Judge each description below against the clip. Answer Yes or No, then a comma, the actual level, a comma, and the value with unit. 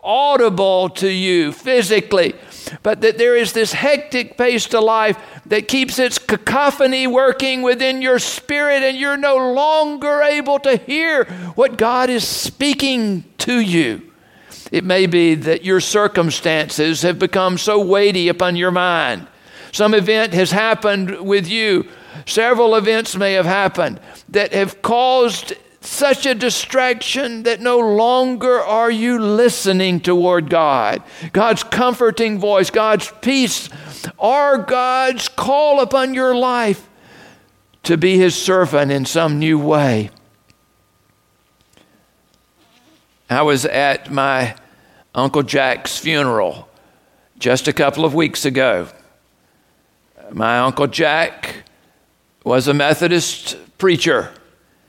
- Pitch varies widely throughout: Yes, wide, 6.7 semitones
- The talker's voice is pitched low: No, high, 210 Hz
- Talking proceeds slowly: Yes, slow, 120 wpm